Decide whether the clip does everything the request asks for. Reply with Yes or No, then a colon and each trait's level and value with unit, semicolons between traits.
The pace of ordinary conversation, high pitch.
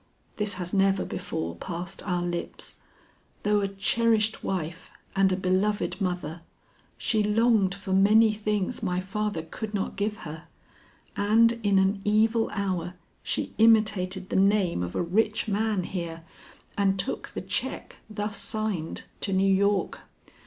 Yes: average, 145 wpm; high, 195 Hz